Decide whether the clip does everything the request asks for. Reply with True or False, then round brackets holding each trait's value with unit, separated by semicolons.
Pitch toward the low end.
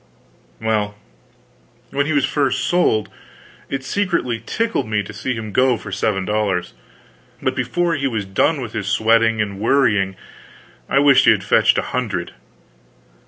True (115 Hz)